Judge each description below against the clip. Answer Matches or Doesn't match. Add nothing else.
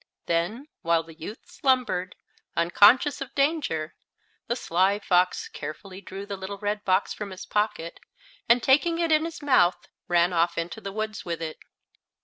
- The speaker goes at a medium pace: Matches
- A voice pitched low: Doesn't match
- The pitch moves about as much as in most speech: Doesn't match